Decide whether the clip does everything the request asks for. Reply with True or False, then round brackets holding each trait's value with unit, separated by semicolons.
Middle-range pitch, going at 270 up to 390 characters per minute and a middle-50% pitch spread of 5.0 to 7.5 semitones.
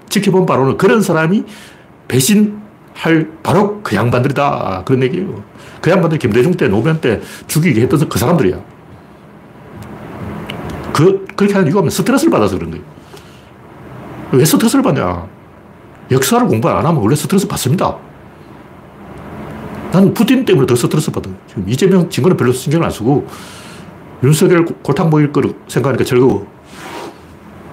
True (170 Hz; 325 characters per minute; 5.7 semitones)